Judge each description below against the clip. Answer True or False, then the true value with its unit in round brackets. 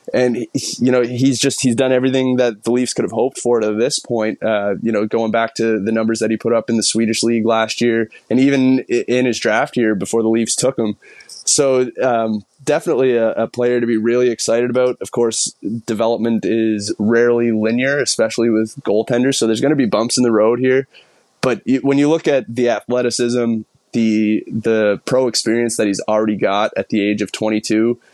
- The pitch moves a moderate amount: False (2.0 semitones)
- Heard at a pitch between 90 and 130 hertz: True (115 Hz)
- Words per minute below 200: False (205 wpm)